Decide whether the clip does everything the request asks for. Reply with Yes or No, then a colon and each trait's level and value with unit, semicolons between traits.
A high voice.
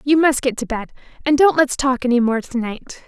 Yes: very high, 260 Hz